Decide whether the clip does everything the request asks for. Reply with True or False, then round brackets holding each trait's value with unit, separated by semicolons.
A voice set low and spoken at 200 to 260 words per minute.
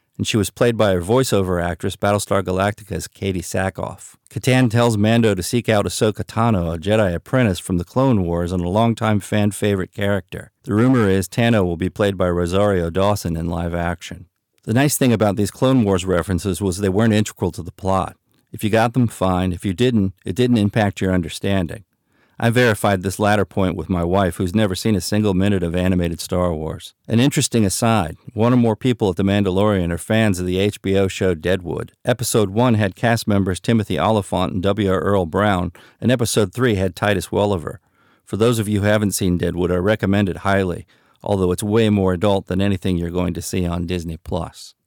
True (100 Hz; 205 wpm)